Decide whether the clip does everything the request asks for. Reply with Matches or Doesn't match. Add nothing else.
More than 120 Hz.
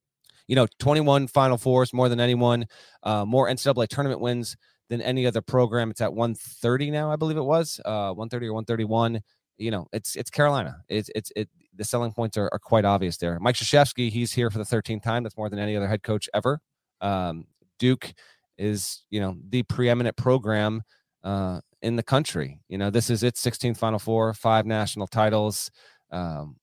Doesn't match